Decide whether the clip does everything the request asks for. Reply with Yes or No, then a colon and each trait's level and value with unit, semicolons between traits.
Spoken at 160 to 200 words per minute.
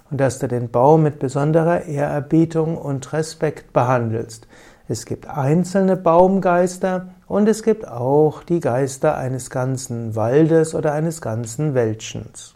No: average, 135 wpm